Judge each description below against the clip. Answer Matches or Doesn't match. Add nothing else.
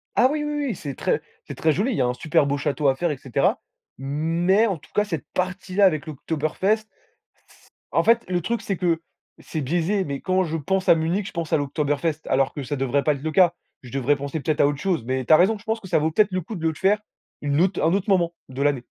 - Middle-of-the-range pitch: Matches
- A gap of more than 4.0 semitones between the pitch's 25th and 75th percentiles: Matches